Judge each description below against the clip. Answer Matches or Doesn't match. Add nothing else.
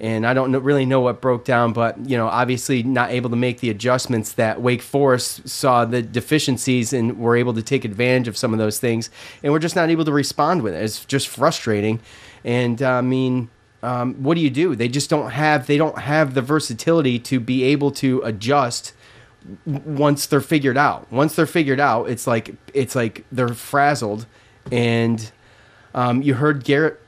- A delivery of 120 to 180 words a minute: Doesn't match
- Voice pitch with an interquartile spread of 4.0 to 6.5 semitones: Doesn't match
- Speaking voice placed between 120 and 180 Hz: Matches